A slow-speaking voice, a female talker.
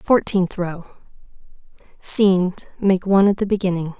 Yes: slow, 105 wpm; female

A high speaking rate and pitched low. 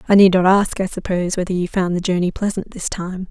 No: fast, 255 wpm; medium, 185 Hz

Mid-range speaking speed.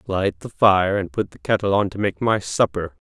No: fast, 235 wpm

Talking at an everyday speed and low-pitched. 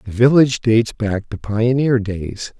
Yes: average, 160 wpm; low, 110 Hz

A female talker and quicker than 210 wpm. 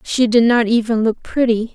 No: female; fast, 205 wpm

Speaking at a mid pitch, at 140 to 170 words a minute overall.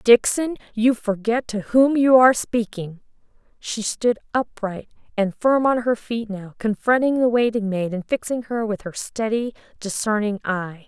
No: high, 225 Hz; average, 160 wpm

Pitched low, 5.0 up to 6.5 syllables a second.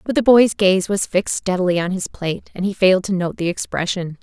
No: high, 190 Hz; 5.9 syllables/s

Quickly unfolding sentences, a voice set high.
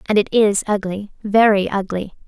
No: slow, 130 wpm; high, 200 Hz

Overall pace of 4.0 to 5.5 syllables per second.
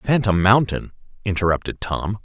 Yes: 4.9 syllables/s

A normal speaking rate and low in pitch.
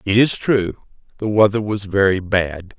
Yes: average, 170 wpm; low, 100 Hz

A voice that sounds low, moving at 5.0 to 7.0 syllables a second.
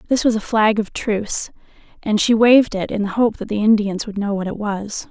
No: high, 210 Hz; 5.5 syllables/s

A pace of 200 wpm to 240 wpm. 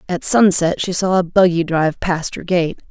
Yes: fast, 205 wpm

